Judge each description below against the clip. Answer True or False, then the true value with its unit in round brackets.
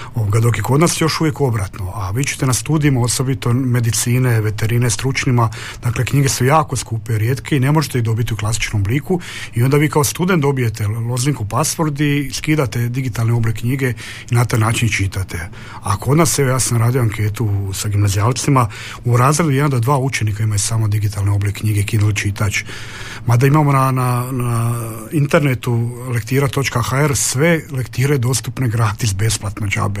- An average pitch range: True (3.6 semitones)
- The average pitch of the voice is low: True (120 Hz)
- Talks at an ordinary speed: False (170 wpm)